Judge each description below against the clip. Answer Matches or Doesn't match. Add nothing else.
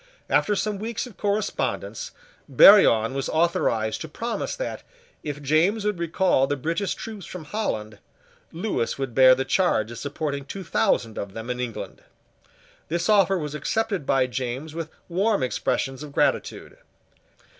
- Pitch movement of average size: Doesn't match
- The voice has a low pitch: Doesn't match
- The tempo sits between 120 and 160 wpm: Matches